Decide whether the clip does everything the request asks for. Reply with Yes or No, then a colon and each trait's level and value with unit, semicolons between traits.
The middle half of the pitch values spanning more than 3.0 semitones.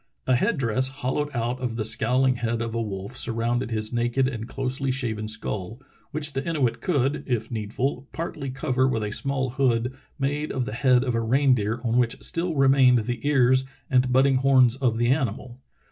No: narrow, 2.6 semitones